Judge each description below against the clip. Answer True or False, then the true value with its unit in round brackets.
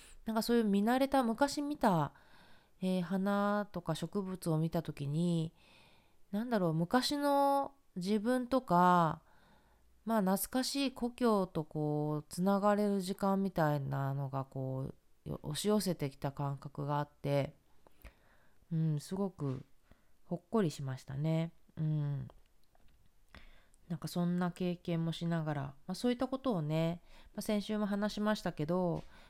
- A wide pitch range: True (5.7 semitones)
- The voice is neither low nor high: True (175 Hz)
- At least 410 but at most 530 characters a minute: False (260 characters per minute)